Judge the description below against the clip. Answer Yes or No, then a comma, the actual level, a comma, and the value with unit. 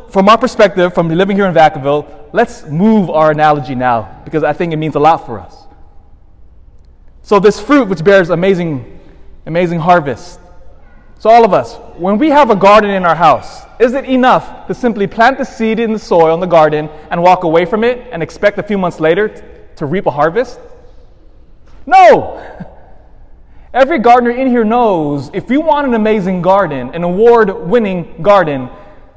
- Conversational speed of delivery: Yes, average, 180 wpm